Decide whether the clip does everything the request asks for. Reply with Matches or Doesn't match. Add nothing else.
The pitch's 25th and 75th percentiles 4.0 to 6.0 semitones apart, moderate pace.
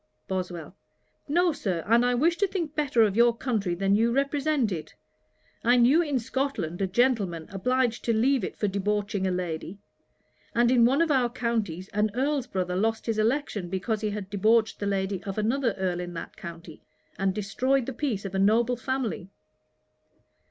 Matches